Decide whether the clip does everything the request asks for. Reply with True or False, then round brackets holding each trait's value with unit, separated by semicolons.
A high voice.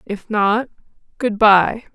True (210 Hz)